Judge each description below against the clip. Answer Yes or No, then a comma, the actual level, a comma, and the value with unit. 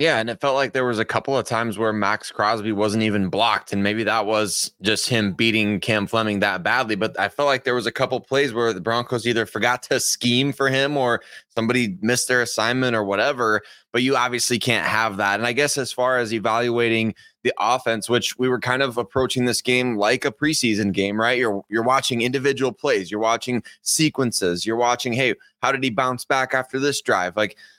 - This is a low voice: Yes, low, 120 Hz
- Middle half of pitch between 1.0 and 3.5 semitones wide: Yes, narrow, 2.6 semitones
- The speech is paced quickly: Yes, fast, 220 wpm